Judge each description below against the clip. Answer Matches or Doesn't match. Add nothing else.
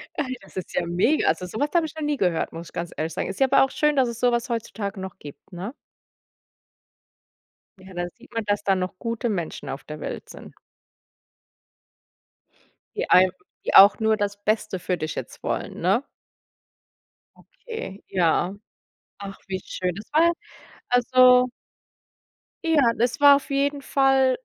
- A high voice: Matches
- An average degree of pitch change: Doesn't match